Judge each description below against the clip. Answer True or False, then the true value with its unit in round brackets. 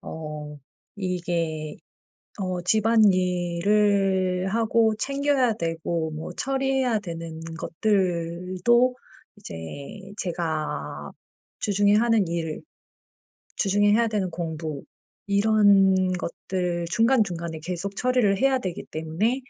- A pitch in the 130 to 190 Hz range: True (185 Hz)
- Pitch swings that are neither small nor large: True (4.5 semitones)